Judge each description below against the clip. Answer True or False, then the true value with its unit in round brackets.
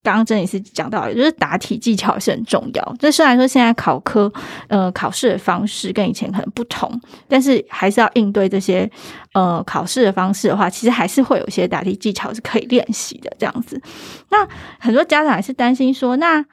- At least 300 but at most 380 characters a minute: True (325 characters per minute)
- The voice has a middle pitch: False (225 Hz)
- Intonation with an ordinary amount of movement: True (4.4 semitones)